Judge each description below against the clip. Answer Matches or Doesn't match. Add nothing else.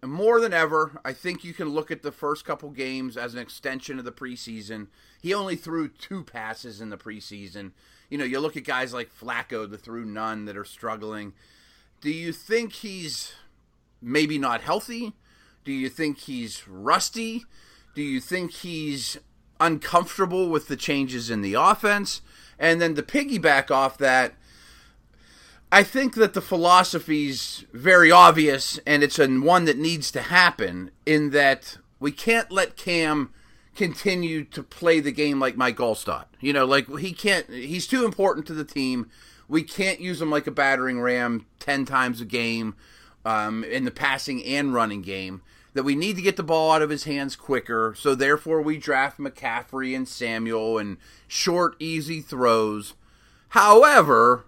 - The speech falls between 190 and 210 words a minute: Doesn't match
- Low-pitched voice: Doesn't match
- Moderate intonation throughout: Doesn't match